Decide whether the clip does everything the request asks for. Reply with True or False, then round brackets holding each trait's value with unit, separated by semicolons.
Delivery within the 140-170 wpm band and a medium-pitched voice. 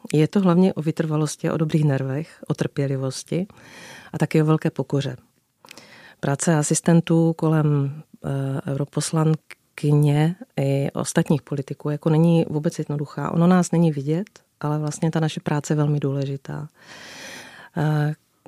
False (130 wpm; 155 Hz)